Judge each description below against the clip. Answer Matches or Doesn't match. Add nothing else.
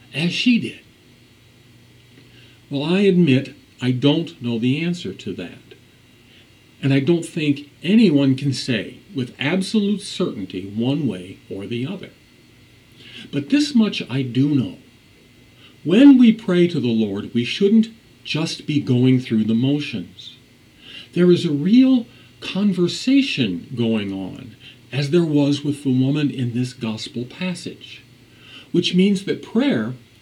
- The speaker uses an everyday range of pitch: Doesn't match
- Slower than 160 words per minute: Matches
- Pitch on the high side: Doesn't match